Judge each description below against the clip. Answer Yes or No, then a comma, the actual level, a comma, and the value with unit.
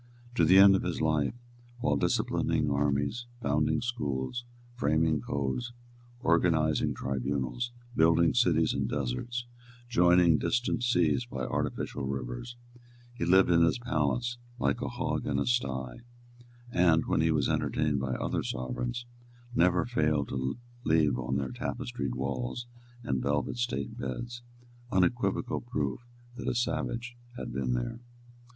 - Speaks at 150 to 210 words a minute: No, slow, 135 wpm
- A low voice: Yes, very low, 80 Hz